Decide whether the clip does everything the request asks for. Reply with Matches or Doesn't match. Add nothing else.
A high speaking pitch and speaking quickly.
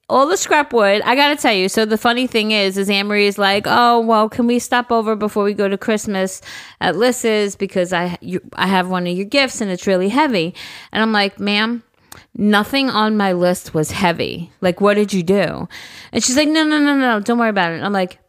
Matches